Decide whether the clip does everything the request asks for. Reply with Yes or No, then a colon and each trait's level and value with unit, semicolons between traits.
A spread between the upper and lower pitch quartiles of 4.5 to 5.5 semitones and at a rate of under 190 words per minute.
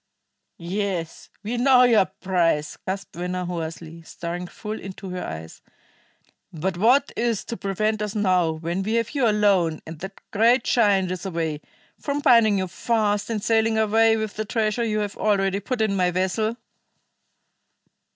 No: average, 3.7 semitones; average, 160 wpm